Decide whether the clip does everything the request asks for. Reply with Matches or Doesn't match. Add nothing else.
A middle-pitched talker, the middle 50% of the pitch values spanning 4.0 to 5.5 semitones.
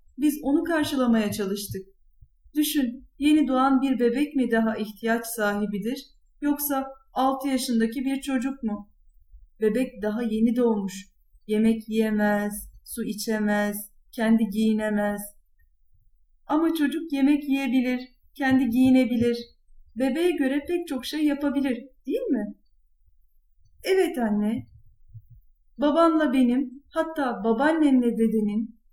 Doesn't match